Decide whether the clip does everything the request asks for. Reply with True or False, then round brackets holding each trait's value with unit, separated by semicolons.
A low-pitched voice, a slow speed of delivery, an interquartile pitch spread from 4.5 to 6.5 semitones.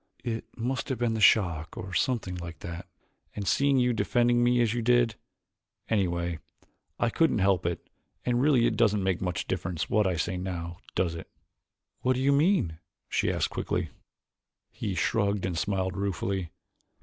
False (100 Hz; 170 wpm; 5.1 semitones)